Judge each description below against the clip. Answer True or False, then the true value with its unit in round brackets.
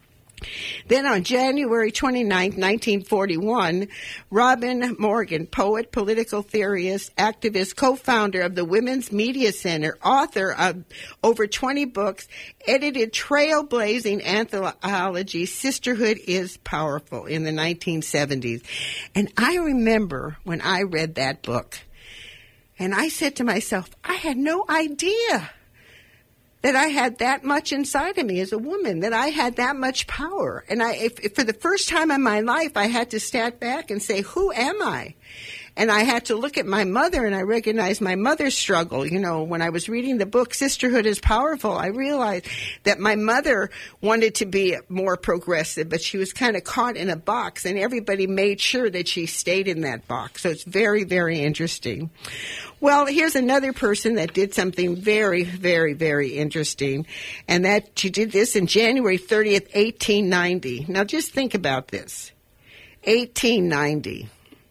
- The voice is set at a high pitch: True (210 Hz)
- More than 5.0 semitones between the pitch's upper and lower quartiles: True (5.5 semitones)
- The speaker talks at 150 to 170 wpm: True (160 wpm)